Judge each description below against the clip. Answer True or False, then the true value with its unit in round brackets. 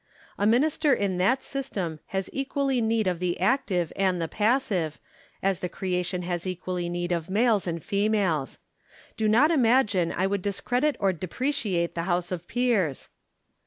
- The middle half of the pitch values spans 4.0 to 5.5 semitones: True (5.2 semitones)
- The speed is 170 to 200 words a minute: False (160 wpm)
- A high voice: True (195 Hz)